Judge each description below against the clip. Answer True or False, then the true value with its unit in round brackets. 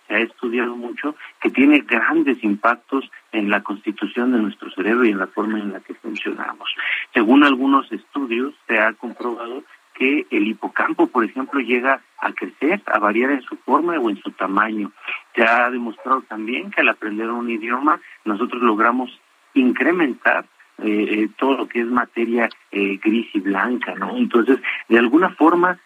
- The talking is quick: False (165 wpm)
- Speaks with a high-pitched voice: False (120 Hz)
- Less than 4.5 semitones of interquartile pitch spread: True (3.9 semitones)